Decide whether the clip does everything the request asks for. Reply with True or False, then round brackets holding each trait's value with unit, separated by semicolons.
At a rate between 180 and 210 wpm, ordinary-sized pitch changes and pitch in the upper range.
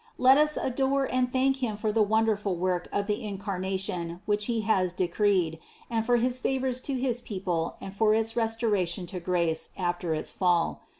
True (185 wpm; 4.9 semitones; 210 Hz)